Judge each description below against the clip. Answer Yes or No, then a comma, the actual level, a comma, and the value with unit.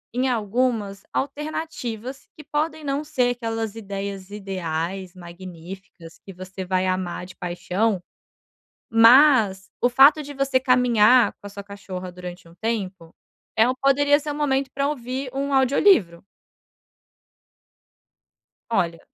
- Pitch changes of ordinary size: No, wide, 6.2 semitones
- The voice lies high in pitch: Yes, high, 225 Hz